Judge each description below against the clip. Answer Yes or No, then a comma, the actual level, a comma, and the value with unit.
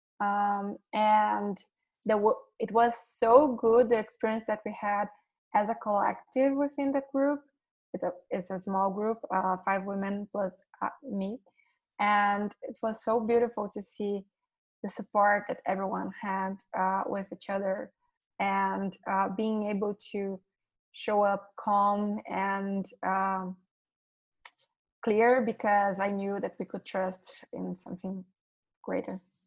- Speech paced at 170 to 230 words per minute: No, slow, 135 wpm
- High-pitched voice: Yes, high, 205 Hz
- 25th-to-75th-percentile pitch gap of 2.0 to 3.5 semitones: Yes, average, 2.8 semitones